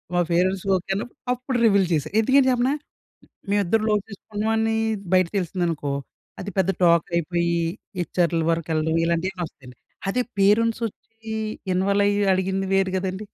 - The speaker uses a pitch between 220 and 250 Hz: No, high, 190 Hz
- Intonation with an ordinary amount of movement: Yes, average, 3.7 semitones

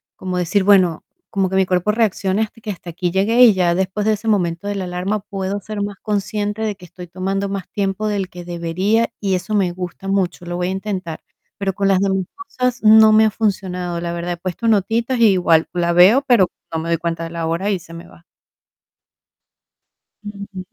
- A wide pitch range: No, average, 2.8 semitones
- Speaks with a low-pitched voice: No, high, 190 Hz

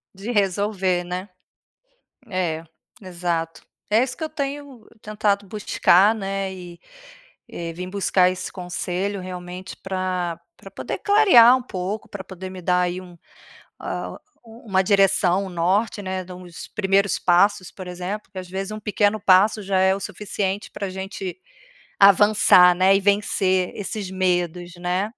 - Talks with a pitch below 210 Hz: Yes, high, 190 Hz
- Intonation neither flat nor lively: No, narrow, 2.1 semitones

